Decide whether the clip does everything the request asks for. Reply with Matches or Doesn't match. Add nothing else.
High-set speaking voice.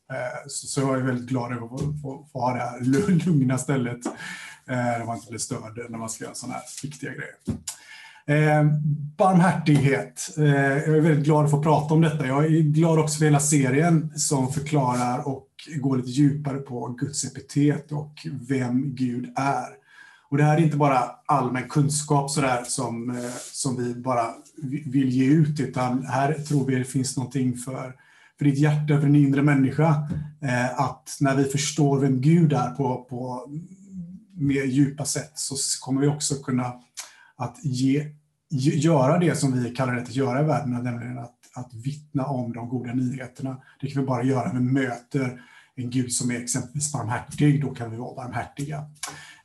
Doesn't match